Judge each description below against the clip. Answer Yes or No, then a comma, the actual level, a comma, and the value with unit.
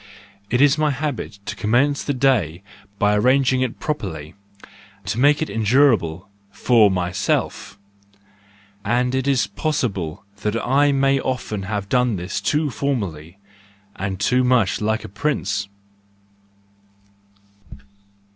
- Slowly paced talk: Yes, slow, 120 wpm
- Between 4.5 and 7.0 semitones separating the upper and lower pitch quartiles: Yes, wide, 5.4 semitones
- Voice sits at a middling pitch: No, low, 120 Hz